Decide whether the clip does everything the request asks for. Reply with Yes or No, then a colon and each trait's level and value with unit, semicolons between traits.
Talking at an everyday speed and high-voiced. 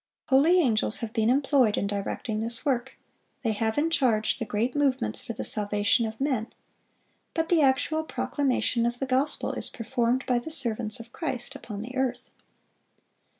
Yes: average, 170 wpm; high, 245 Hz